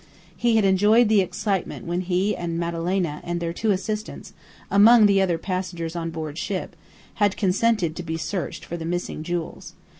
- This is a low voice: No, medium, 180 Hz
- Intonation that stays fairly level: No, average, 3.3 semitones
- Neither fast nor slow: Yes, average, 175 wpm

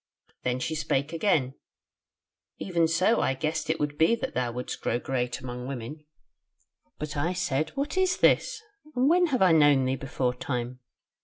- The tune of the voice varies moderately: No, wide, 5.7 semitones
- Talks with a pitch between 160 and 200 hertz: No, medium, 150 Hz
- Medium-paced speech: Yes, average, 170 wpm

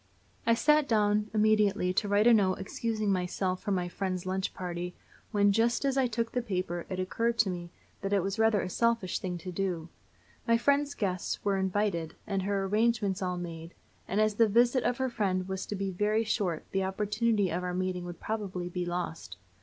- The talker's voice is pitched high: Yes, high, 195 Hz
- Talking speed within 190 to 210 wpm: Yes, average, 200 wpm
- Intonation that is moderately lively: Yes, average, 3.3 semitones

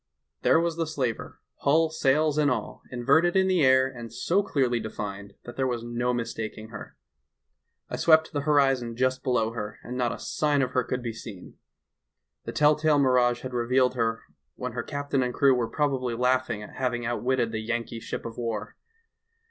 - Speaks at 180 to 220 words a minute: Yes, average, 190 wpm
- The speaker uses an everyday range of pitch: Yes, average, 3.3 semitones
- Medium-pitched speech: No, low, 125 Hz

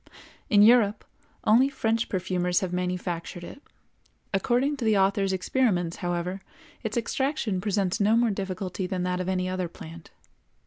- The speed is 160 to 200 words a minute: No, average, 145 wpm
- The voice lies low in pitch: No, high, 190 Hz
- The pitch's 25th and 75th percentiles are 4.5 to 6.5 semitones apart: No, average, 3.6 semitones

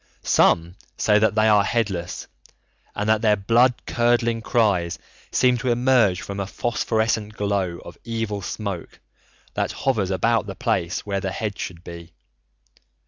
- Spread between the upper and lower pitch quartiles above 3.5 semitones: No, average, 3.1 semitones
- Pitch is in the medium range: No, low, 105 Hz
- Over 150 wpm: No, average, 145 wpm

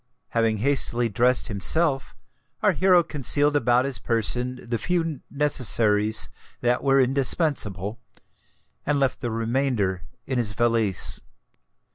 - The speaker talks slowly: Yes, slow, 115 wpm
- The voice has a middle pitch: No, low, 125 Hz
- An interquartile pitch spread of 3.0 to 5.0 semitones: Yes, average, 3.6 semitones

